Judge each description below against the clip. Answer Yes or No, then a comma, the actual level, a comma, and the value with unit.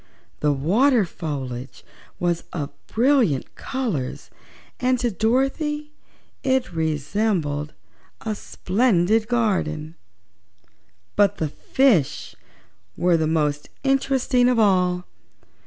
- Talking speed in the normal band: No, slow, 90 wpm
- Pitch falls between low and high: No, high, 195 Hz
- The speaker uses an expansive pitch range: Yes, wide, 8.2 semitones